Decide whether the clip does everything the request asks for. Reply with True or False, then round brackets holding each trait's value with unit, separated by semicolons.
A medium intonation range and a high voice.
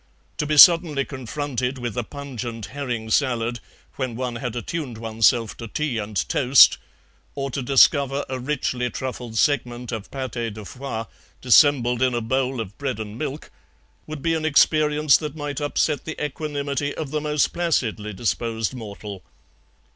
False (3.8 semitones; 130 Hz)